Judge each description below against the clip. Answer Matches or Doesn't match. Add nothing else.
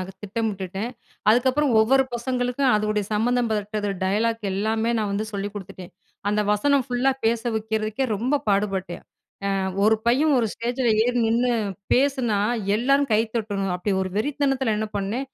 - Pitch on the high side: Matches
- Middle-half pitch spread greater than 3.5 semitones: Doesn't match